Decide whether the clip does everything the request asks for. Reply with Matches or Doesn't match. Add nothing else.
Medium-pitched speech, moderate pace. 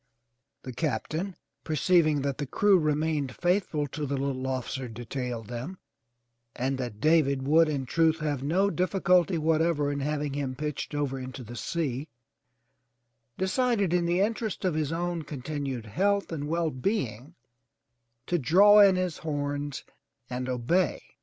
Matches